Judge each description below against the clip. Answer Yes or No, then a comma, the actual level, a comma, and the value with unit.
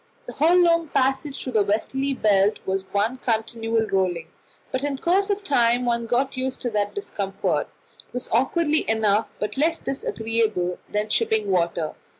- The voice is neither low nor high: No, high, 230 Hz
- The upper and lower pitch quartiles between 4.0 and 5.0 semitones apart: Yes, average, 4.7 semitones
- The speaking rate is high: No, average, 165 wpm